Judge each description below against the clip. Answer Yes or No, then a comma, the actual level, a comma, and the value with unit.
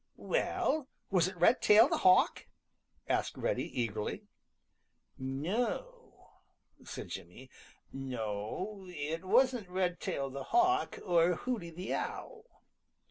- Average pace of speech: No, slow, 100 wpm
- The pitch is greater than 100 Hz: Yes, medium, 185 Hz